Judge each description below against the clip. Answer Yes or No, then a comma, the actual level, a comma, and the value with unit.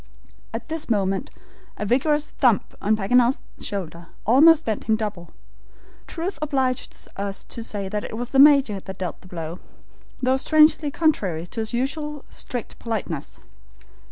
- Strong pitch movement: Yes, wide, 6.1 semitones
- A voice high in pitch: Yes, high, 230 Hz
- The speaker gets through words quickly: No, average, 145 wpm